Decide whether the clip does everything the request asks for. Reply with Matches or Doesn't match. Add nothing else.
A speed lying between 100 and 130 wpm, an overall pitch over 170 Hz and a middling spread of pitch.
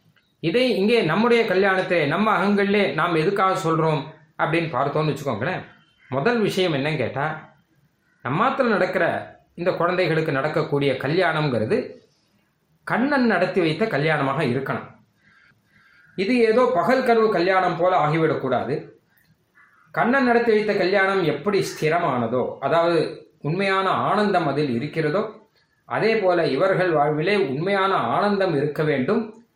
Matches